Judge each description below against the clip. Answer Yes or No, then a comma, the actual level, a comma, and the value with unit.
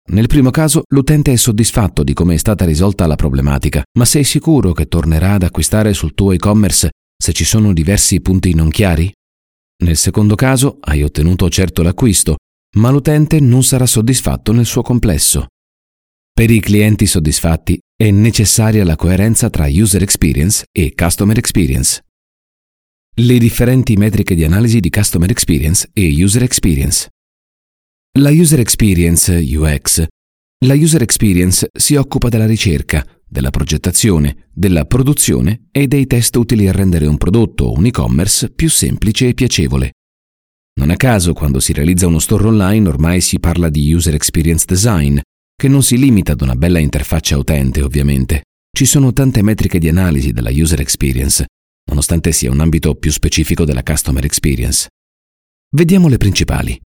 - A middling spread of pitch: No, wide, 6.8 semitones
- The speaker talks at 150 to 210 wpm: Yes, average, 155 wpm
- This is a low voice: Yes, very low, 90 Hz